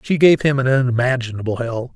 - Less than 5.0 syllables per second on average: No, 6.0 syllables/s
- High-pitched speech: No, low, 130 Hz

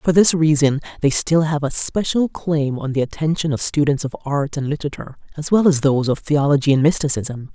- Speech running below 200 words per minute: No, fast, 205 wpm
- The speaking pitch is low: No, medium, 150 Hz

